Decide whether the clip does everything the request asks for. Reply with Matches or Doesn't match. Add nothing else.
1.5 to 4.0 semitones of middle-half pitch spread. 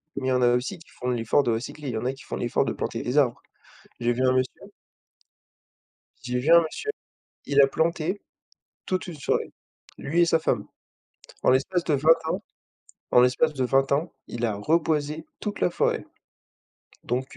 Doesn't match